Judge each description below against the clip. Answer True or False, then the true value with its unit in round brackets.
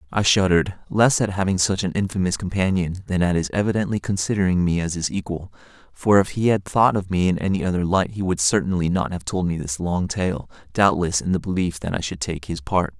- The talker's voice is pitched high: False (90 Hz)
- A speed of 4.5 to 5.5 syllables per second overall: False (5.8 syllables/s)